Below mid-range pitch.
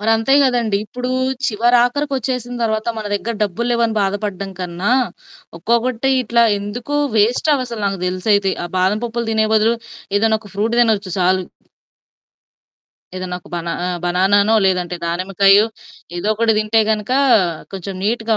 No: high, 215 Hz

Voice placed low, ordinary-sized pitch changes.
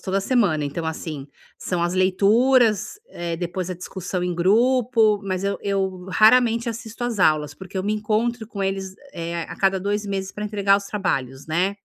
No: high, 195 Hz; average, 3.3 semitones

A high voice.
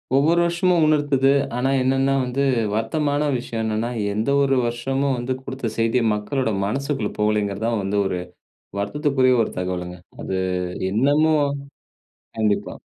No: low, 130 Hz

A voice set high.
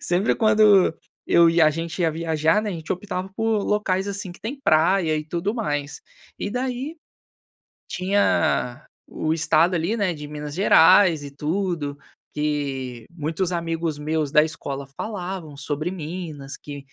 No: medium, 165 Hz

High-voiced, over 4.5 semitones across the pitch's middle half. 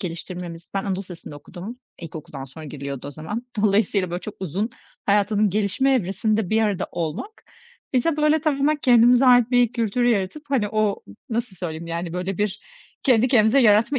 Yes: high, 210 Hz; wide, 5.4 semitones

